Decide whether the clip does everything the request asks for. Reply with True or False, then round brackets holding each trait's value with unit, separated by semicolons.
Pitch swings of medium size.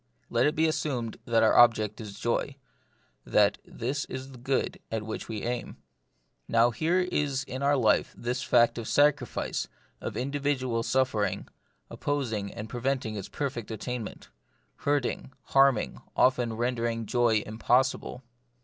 True (3.2 semitones)